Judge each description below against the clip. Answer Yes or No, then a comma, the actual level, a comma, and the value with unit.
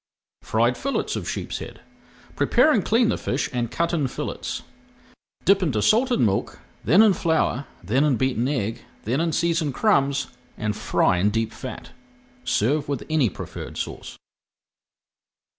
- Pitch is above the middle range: No, medium, 140 Hz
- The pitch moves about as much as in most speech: No, wide, 6.3 semitones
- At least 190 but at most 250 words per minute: No, average, 145 wpm